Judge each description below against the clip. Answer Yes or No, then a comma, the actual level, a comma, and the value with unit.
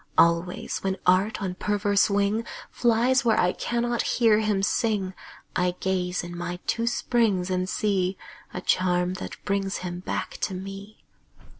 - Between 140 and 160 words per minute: Yes, average, 150 wpm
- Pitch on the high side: Yes, high, 195 Hz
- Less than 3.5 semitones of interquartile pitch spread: Yes, average, 3.0 semitones